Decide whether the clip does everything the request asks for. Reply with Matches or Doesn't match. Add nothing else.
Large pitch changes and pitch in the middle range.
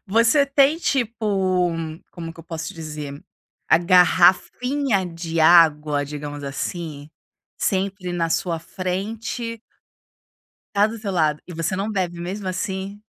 Doesn't match